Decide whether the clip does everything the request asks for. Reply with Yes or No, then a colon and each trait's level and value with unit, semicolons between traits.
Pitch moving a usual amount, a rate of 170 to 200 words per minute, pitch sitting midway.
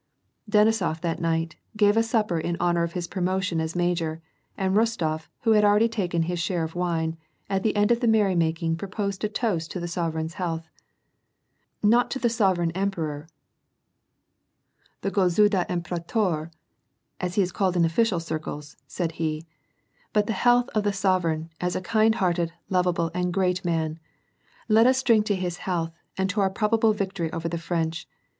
Yes: average, 3.9 semitones; average, 175 wpm; medium, 180 Hz